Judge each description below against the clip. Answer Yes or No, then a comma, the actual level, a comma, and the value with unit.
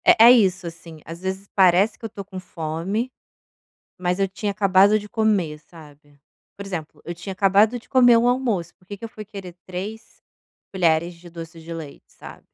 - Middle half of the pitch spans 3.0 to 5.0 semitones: Yes, average, 3.8 semitones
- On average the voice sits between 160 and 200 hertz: Yes, high, 190 Hz